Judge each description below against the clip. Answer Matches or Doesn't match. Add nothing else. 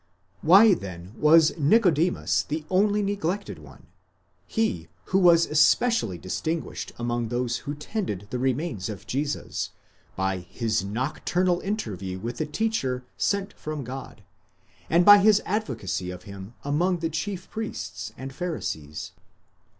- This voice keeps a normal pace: Doesn't match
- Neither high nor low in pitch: Matches